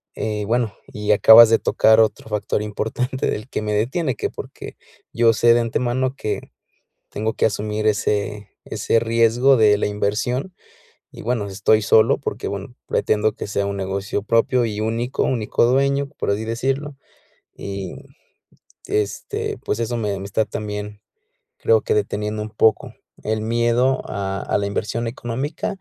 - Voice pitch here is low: Yes, low, 110 Hz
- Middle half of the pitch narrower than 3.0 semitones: Yes, narrow, 2.4 semitones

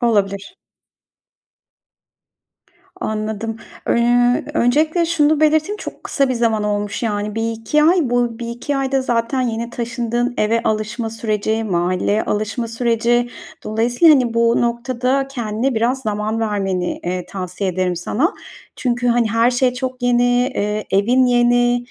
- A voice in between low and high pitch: No, high, 235 Hz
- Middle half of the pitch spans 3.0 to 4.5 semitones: No, narrow, 2.5 semitones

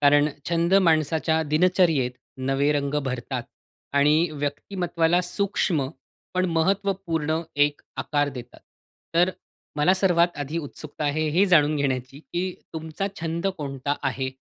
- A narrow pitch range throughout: No, average, 3.3 semitones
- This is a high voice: No, medium, 155 Hz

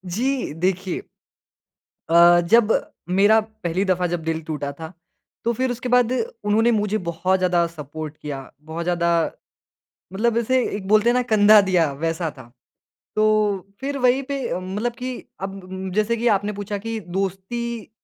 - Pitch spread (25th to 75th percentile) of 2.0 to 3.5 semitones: No, average, 5.0 semitones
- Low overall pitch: No, high, 195 Hz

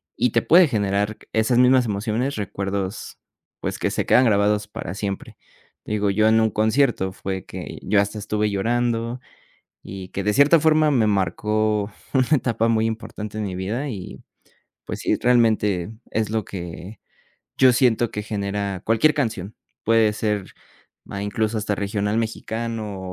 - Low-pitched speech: Yes, low, 110 Hz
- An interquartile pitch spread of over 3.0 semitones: No, narrow, 2.5 semitones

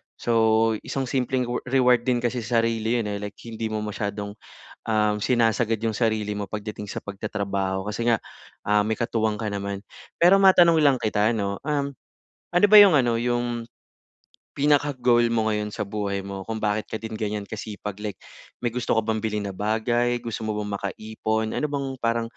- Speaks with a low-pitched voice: Yes, low, 110 Hz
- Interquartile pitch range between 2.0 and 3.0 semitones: Yes, narrow, 2.4 semitones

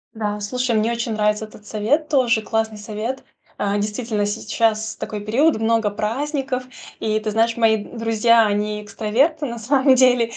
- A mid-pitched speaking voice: No, high, 225 Hz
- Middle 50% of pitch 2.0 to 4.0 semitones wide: Yes, average, 2.7 semitones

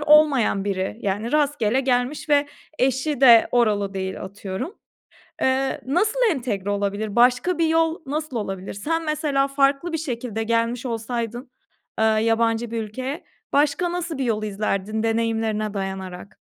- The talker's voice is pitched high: Yes, high, 240 Hz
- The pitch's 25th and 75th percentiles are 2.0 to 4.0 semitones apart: No, average, 5.1 semitones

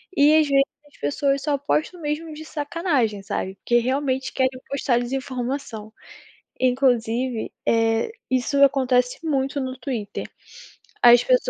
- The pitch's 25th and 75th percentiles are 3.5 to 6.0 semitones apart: No, average, 3.0 semitones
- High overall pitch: Yes, very high, 265 Hz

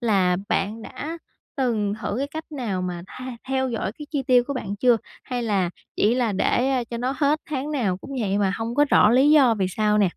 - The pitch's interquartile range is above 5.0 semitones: No, average, 4.7 semitones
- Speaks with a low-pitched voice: No, high, 235 Hz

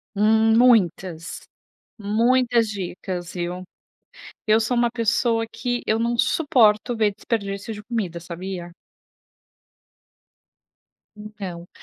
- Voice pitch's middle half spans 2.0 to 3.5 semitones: No, average, 3.9 semitones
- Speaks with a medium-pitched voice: No, high, 215 Hz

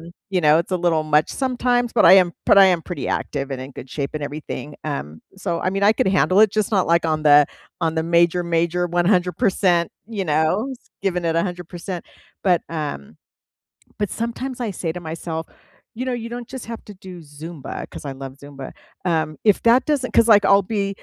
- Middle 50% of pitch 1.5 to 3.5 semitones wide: No, average, 4.4 semitones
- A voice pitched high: No, medium, 175 Hz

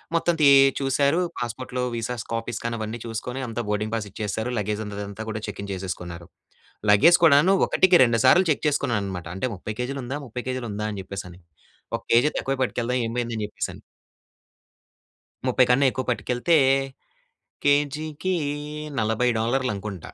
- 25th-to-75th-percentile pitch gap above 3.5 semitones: Yes, average, 4.1 semitones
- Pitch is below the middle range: Yes, low, 120 Hz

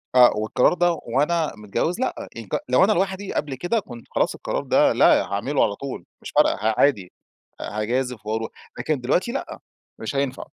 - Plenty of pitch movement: Yes, wide, 7.5 semitones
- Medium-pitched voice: No, low, 130 Hz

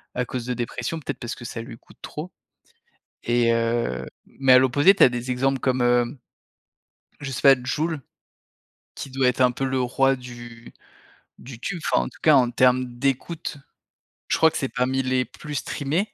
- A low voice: Yes, low, 130 Hz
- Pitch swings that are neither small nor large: No, narrow, 2.1 semitones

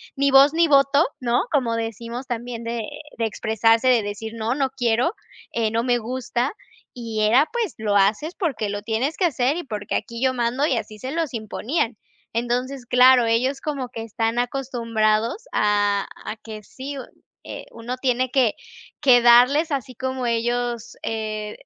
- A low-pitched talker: No, high, 240 Hz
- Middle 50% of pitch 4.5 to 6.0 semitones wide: No, average, 2.8 semitones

